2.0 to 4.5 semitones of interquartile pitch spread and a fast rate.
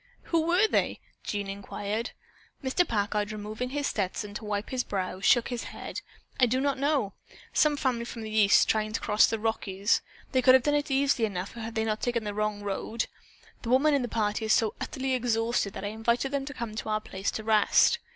Yes: average, 3.7 semitones; fast, 220 wpm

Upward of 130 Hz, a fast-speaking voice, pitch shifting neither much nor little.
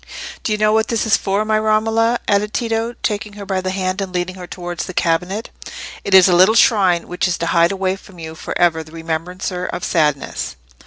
Yes: high, 190 Hz; fast, 220 wpm; average, 3.3 semitones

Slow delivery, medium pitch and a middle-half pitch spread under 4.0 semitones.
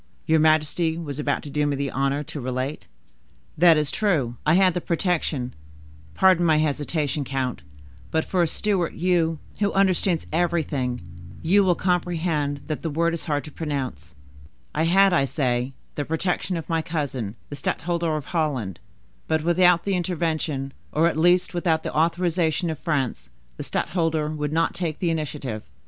No: average, 160 wpm; medium, 155 Hz; average, 3.5 semitones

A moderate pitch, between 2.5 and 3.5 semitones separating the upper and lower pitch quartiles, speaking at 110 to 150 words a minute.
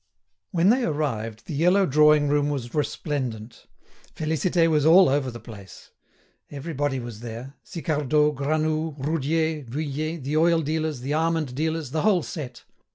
Yes: medium, 150 Hz; average, 3.2 semitones; average, 145 wpm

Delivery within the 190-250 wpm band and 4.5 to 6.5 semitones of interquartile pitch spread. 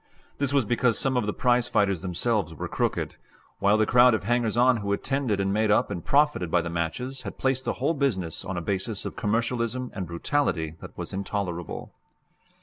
Yes: average, 200 wpm; average, 4.9 semitones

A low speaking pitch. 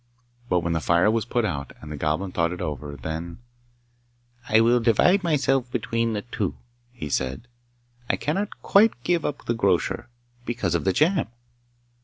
Yes: low, 110 Hz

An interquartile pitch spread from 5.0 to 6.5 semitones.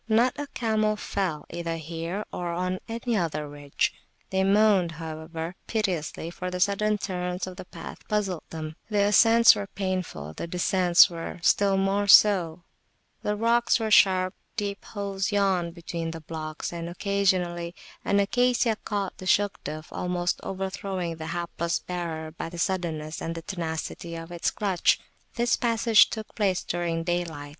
No: average, 3.4 semitones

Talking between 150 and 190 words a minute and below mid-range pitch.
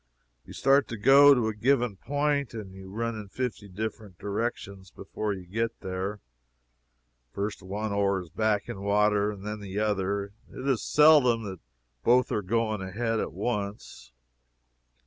Yes: average, 155 wpm; low, 105 Hz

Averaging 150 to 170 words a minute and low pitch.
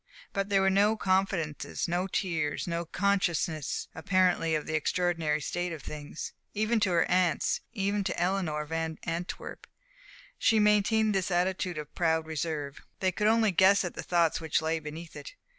No: average, 165 wpm; medium, 175 Hz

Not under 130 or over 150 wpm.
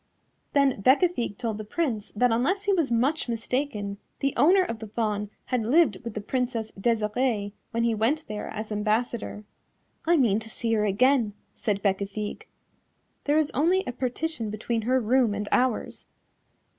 No: average, 165 wpm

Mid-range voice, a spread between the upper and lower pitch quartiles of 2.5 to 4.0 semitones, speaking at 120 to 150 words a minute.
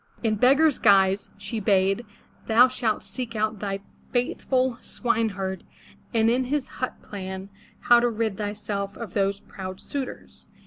No: high, 215 Hz; average, 3.6 semitones; average, 140 wpm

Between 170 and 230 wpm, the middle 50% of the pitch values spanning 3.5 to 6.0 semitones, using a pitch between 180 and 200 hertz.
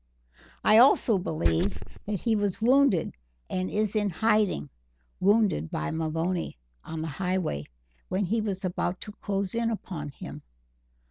No: average, 140 wpm; average, 4.7 semitones; high, 190 Hz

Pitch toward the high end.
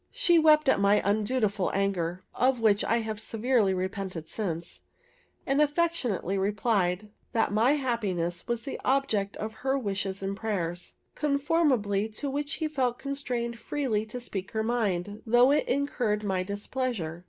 Yes: high, 220 Hz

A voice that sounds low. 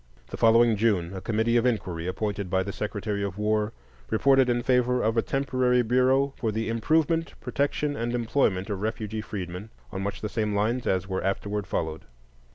Yes: low, 110 Hz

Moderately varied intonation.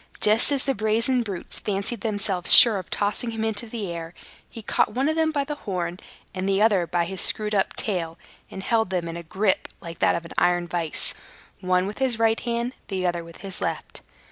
Yes: average, 4.3 semitones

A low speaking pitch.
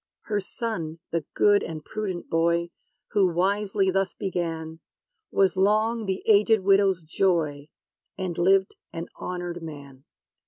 No: medium, 185 Hz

